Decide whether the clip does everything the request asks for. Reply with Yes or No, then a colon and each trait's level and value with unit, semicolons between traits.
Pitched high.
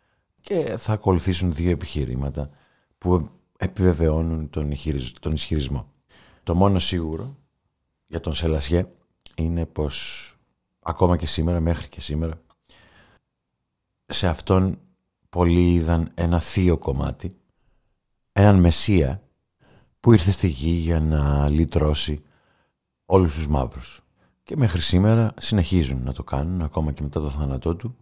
No: very low, 85 Hz